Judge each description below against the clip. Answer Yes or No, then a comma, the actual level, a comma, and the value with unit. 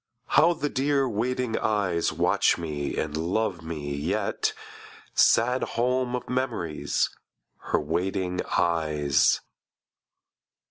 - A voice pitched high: No, very low, 95 Hz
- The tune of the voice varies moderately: No, wide, 7.7 semitones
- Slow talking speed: Yes, slow, 100 wpm